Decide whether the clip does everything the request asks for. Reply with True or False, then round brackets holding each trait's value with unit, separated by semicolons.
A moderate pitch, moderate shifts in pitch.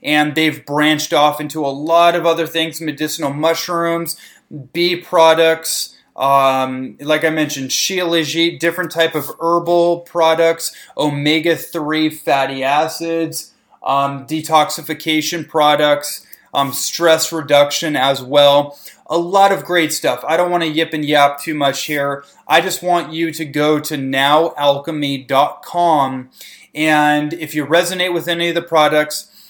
False (155 Hz; 2.2 semitones)